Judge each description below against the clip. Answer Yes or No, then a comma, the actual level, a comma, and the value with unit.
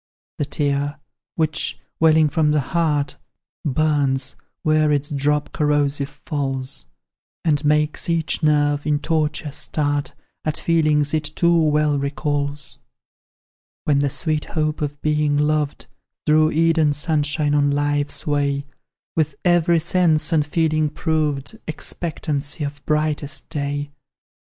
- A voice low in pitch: No, medium, 150 Hz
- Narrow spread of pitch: Yes, narrow, 1.3 semitones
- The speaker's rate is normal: No, slow, 120 wpm